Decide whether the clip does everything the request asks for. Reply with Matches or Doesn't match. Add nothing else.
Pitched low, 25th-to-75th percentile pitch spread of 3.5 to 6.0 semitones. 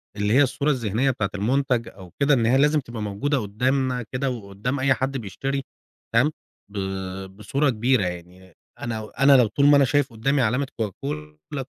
Matches